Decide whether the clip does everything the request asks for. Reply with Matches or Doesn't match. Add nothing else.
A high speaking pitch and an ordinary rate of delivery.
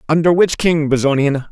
Doesn't match